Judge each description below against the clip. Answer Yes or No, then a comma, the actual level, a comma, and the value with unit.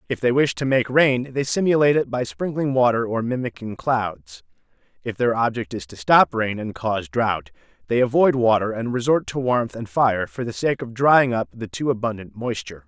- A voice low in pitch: Yes, low, 120 Hz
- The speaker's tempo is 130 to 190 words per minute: No, fast, 205 wpm